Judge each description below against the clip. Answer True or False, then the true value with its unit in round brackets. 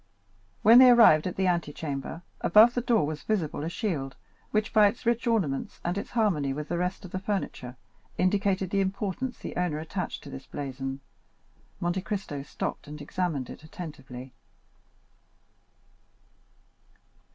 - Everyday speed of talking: True (150 wpm)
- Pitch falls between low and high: True (180 Hz)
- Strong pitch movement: True (5.8 semitones)